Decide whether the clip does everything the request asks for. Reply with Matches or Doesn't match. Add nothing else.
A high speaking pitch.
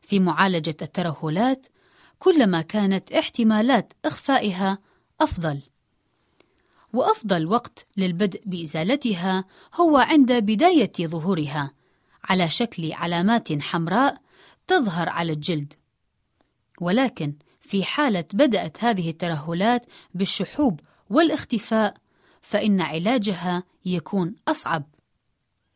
Matches